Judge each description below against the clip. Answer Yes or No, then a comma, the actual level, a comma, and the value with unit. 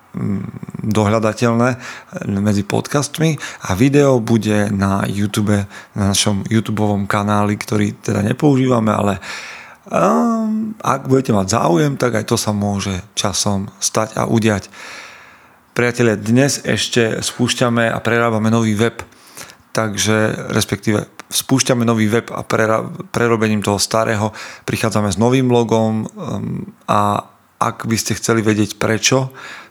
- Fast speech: No, average, 120 wpm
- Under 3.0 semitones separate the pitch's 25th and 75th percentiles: Yes, narrow, 2.5 semitones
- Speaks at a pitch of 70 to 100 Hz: No, low, 110 Hz